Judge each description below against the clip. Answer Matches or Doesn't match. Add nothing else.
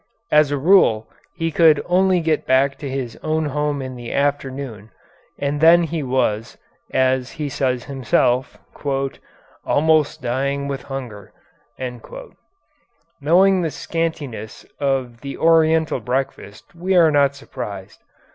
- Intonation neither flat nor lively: Matches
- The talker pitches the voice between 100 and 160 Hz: Matches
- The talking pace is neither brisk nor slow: Doesn't match